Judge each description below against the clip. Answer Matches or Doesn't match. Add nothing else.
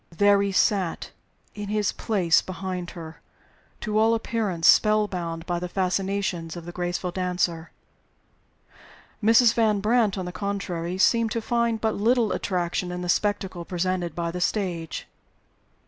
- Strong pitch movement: Doesn't match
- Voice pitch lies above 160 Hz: Matches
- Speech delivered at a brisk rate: Doesn't match